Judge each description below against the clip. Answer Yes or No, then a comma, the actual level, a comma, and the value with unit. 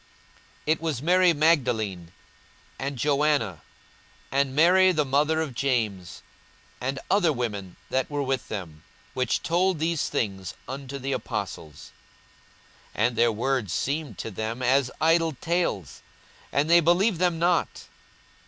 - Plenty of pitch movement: Yes, wide, 5.9 semitones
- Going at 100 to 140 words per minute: Yes, slow, 135 wpm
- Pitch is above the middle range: No, medium, 140 Hz